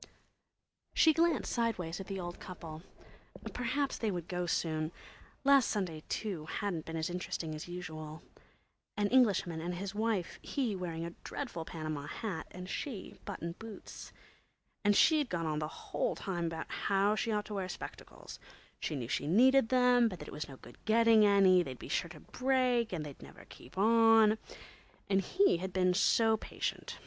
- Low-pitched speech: No, high, 190 Hz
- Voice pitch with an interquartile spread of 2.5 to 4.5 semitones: No, wide, 5.5 semitones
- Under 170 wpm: No, average, 175 wpm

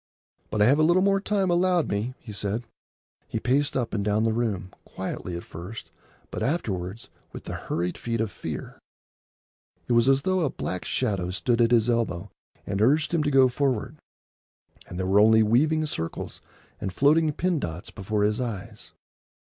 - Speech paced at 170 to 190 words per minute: Yes, average, 180 wpm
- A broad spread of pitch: Yes, wide, 6.1 semitones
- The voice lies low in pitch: Yes, low, 115 Hz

